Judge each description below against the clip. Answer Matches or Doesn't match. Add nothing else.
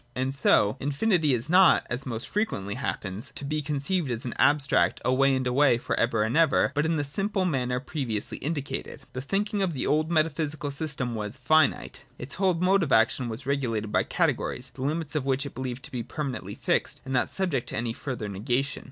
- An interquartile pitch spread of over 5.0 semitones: Doesn't match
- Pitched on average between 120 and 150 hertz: Matches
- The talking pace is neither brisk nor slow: Doesn't match